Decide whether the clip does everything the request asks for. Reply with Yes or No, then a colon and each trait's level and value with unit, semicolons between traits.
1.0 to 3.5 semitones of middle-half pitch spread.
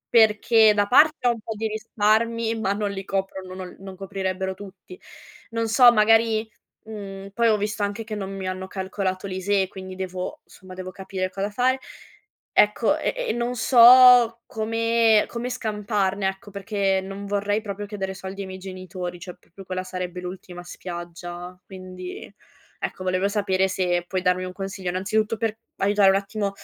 Yes: narrow, 2.6 semitones